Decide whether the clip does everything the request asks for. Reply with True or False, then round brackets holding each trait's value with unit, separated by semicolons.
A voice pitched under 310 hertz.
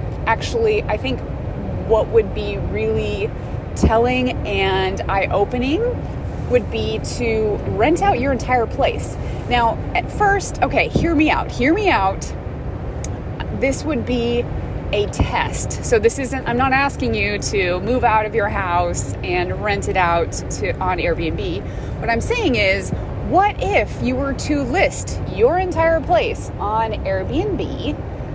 False (330 Hz)